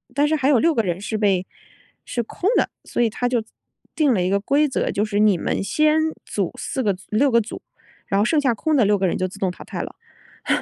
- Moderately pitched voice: No, high, 225 Hz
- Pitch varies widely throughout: Yes, wide, 6.0 semitones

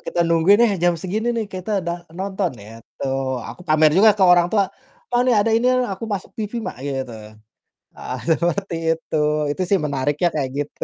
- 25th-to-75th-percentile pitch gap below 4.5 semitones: No, average, 4.9 semitones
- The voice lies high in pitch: No, medium, 175 Hz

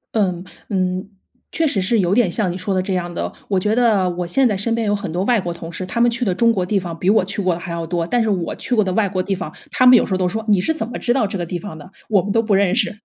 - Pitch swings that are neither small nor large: Yes, average, 3.5 semitones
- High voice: Yes, high, 195 Hz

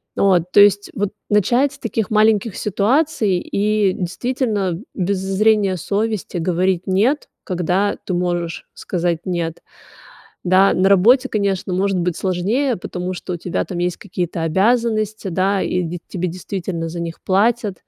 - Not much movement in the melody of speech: No, average, 3.1 semitones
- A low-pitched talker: No, high, 190 Hz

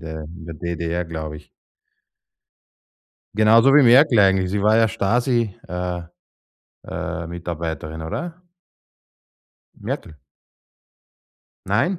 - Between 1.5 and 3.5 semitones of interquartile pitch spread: No, wide, 5.6 semitones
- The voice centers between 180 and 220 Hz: No, very low, 90 Hz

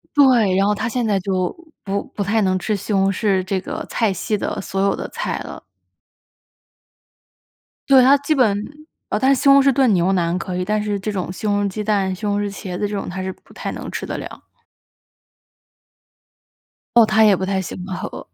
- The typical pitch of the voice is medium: No, high, 205 Hz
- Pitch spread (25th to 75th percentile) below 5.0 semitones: Yes, narrow, 2.6 semitones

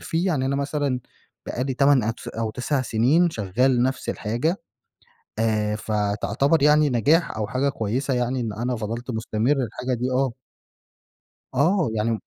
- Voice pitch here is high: No, low, 125 Hz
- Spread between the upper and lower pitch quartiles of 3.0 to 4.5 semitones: Yes, average, 3.9 semitones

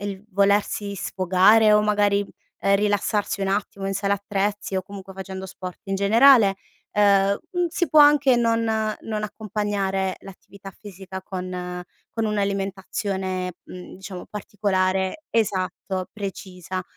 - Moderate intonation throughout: No, narrow, 1.8 semitones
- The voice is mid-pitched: No, high, 200 Hz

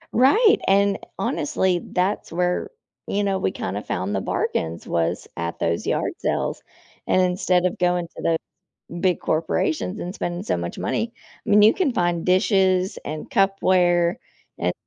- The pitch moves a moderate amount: Yes, average, 3.0 semitones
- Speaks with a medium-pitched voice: Yes, medium, 180 Hz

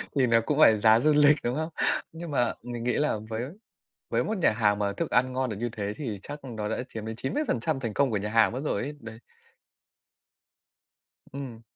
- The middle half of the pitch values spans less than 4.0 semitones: No, average, 4.4 semitones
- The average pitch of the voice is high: No, low, 120 Hz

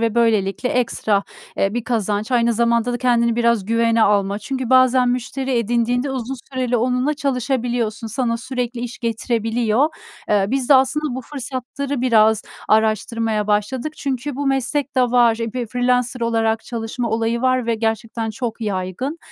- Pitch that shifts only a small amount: Yes, narrow, 2.3 semitones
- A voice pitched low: No, high, 235 Hz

